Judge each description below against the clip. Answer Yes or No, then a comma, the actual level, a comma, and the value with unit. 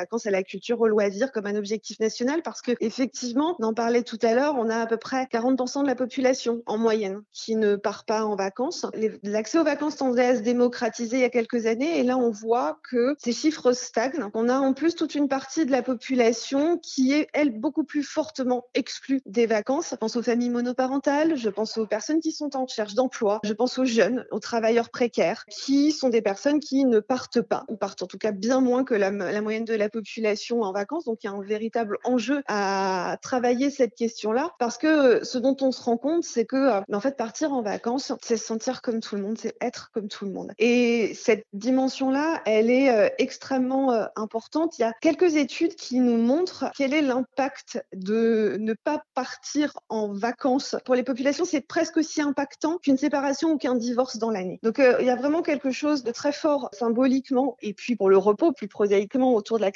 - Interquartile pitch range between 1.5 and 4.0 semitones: Yes, average, 3.5 semitones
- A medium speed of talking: No, fast, 225 wpm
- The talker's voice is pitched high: Yes, high, 245 Hz